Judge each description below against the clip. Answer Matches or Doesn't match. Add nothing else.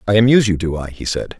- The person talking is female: Doesn't match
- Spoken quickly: Matches